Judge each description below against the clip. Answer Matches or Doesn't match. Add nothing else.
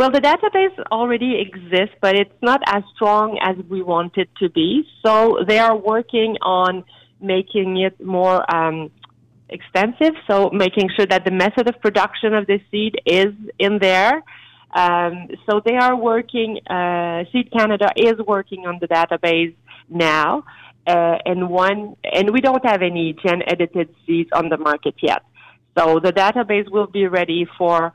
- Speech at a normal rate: Matches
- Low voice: Doesn't match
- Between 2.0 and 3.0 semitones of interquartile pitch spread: Doesn't match